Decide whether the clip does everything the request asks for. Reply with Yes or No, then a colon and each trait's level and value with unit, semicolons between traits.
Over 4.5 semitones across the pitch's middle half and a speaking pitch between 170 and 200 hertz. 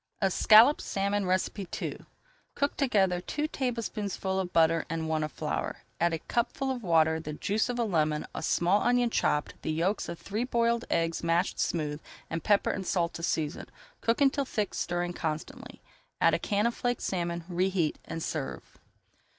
Yes: wide, 5.6 semitones; medium, 185 Hz